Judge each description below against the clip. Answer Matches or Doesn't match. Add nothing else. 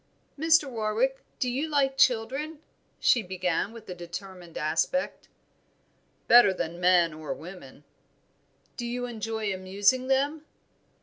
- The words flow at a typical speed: Doesn't match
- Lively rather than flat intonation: Matches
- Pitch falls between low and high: Doesn't match